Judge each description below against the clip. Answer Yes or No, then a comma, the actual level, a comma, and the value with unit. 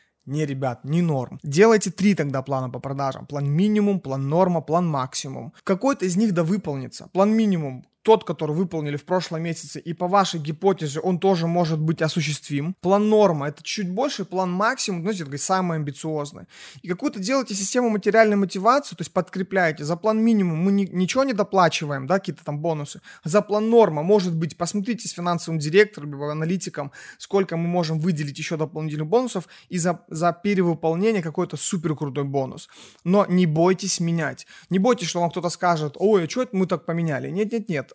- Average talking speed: No, fast, 180 wpm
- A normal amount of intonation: Yes, average, 4.2 semitones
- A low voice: No, medium, 175 Hz